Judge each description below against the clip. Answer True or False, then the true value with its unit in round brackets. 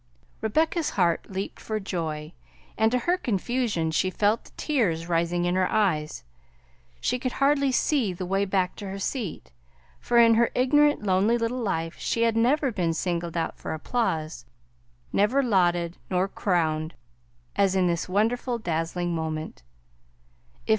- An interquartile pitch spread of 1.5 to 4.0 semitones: False (5.6 semitones)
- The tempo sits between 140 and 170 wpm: True (150 wpm)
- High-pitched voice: True (195 Hz)